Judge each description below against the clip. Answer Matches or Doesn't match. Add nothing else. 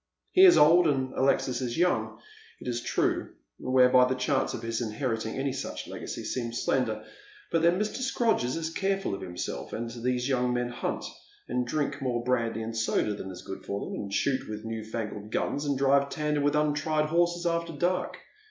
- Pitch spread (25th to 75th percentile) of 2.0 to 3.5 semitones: Doesn't match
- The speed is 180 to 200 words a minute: Matches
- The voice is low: Matches